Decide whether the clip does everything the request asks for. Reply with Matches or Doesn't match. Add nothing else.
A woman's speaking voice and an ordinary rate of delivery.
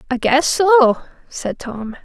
Matches